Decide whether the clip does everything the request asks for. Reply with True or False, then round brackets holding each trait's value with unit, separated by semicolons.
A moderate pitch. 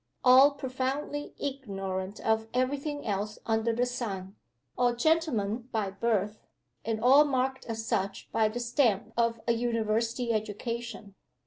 False (230 Hz)